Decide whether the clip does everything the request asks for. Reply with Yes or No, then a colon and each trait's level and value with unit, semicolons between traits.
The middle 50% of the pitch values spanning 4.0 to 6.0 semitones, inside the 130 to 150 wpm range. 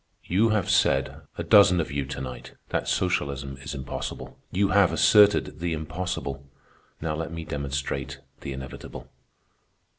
Yes: average, 4.6 semitones; average, 145 wpm